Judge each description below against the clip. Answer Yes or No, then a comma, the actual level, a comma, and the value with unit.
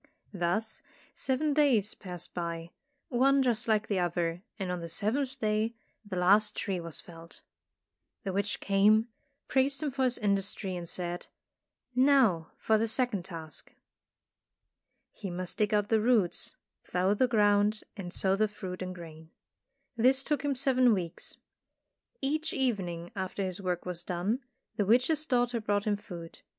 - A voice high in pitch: Yes, high, 205 Hz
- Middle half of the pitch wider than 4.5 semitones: Yes, average, 5.2 semitones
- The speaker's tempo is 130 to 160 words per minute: Yes, average, 155 wpm